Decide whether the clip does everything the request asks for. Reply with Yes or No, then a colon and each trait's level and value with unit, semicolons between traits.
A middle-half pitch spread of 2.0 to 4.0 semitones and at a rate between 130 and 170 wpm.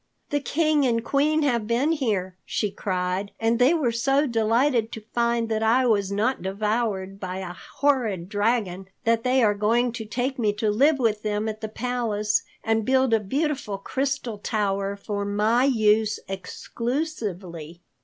Yes: average, 3.6 semitones; average, 165 wpm